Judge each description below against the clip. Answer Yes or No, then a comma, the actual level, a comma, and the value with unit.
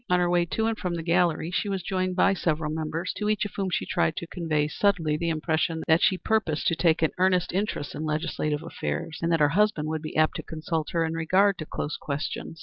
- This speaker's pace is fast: Yes, fast, 240 wpm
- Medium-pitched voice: Yes, medium, 165 Hz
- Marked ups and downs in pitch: No, average, 2.8 semitones